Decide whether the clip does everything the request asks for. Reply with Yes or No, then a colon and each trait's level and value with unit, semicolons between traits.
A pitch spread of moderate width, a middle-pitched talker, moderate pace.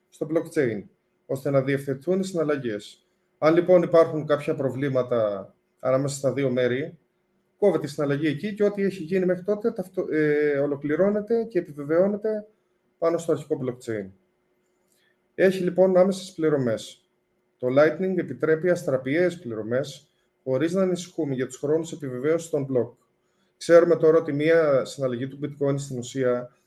Yes: average, 4.9 semitones; medium, 155 Hz; average, 135 wpm